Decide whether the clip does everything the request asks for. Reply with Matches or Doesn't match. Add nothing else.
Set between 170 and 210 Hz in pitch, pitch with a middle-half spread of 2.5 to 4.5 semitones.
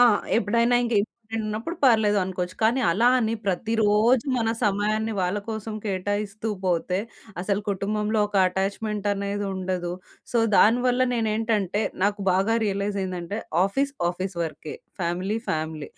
Matches